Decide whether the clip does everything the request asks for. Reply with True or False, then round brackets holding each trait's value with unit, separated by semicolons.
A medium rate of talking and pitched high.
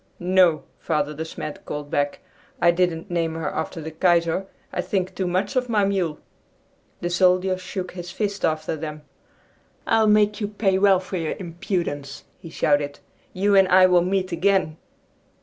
False (165 wpm; 180 Hz)